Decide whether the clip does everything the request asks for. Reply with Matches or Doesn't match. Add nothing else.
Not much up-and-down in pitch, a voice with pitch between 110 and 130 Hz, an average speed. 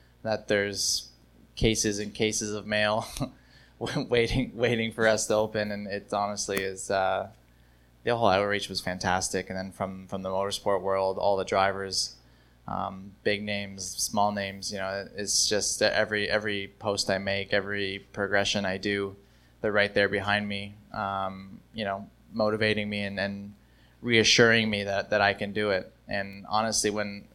Doesn't match